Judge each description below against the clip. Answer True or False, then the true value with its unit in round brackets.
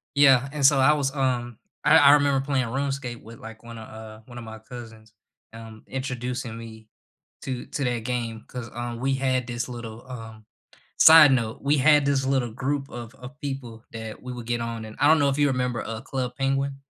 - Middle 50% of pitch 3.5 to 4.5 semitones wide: False (3.0 semitones)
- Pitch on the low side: True (125 Hz)